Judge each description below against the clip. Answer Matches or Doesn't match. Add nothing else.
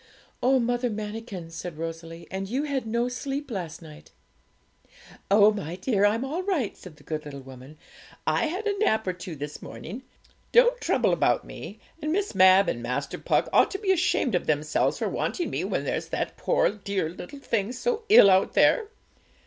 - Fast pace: Doesn't match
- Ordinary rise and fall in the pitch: Doesn't match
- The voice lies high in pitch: Matches